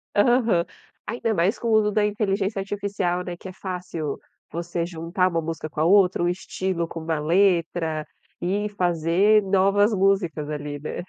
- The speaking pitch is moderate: Yes, medium, 180 Hz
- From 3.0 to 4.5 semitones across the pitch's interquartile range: Yes, average, 3.3 semitones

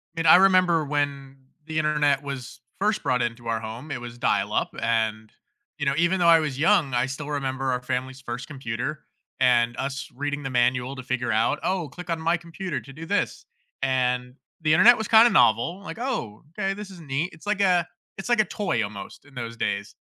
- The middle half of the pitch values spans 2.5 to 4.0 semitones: No, wide, 5.4 semitones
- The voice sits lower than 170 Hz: Yes, medium, 140 Hz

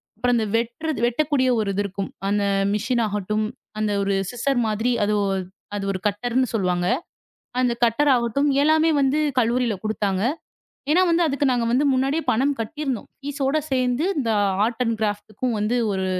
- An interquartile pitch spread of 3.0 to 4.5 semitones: Yes, average, 4.2 semitones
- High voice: Yes, high, 240 Hz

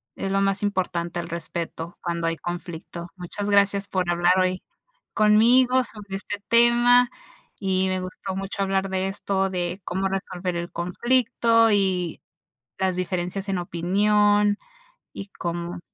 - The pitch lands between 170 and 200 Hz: Yes, high, 190 Hz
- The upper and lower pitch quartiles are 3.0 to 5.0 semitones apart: No, narrow, 2.6 semitones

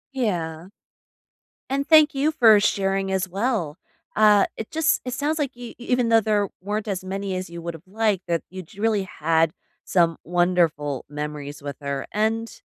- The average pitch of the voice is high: Yes, high, 195 Hz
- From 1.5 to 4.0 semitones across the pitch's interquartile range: No, average, 5.2 semitones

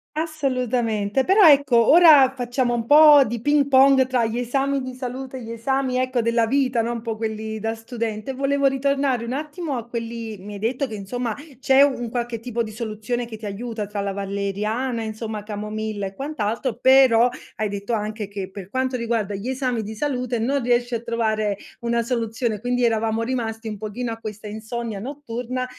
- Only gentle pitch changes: No, average, 3.1 semitones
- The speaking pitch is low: No, high, 235 Hz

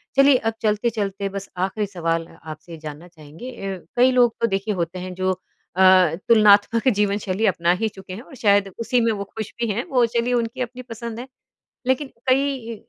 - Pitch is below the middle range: No, high, 210 Hz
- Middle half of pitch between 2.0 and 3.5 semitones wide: No, average, 4.2 semitones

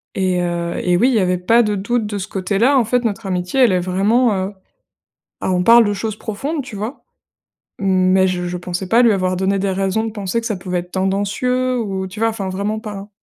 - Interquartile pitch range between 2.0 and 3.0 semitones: No, average, 3.4 semitones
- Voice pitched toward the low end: No, high, 200 Hz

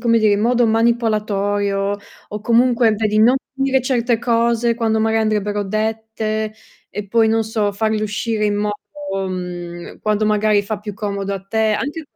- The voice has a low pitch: No, high, 215 Hz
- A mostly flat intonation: Yes, narrow, 1.9 semitones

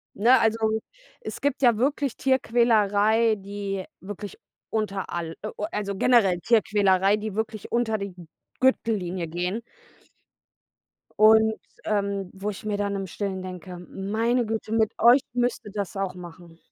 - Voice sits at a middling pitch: No, high, 205 Hz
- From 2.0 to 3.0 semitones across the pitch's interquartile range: Yes, average, 2.7 semitones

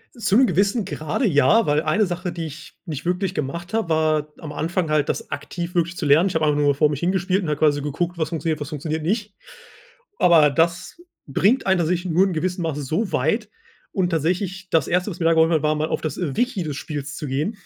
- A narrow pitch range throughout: No, average, 3.4 semitones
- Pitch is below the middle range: No, medium, 165 Hz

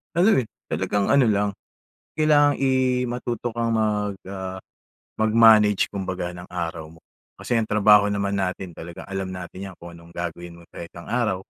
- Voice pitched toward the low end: Yes, low, 100 Hz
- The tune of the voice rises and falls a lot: No, average, 4.5 semitones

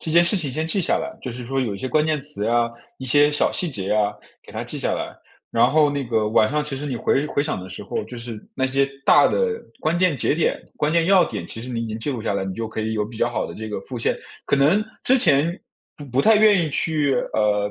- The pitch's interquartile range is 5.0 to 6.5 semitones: Yes, wide, 5.5 semitones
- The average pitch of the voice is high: No, low, 135 Hz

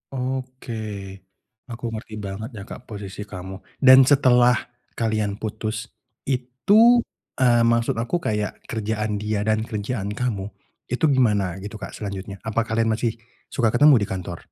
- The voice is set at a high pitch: No, low, 110 Hz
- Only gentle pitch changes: No, average, 3.2 semitones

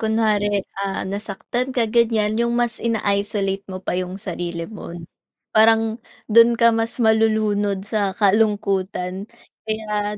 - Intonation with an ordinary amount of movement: No, narrow, 2.2 semitones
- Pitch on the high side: Yes, high, 210 Hz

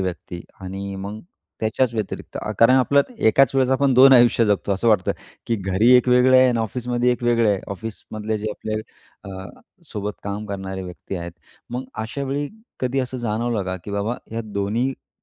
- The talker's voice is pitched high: No, low, 110 Hz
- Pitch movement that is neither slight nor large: Yes, average, 3.9 semitones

